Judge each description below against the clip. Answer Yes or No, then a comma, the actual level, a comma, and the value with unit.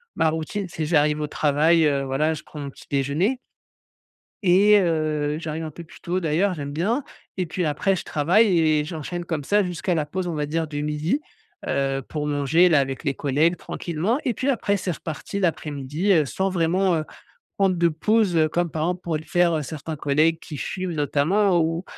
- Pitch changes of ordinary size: Yes, average, 3.3 semitones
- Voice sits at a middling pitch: Yes, medium, 160 Hz